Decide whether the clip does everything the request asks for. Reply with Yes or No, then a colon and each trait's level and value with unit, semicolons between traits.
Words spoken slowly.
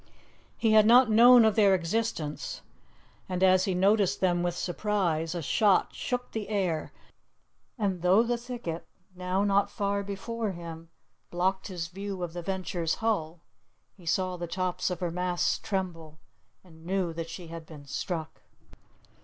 No: average, 155 wpm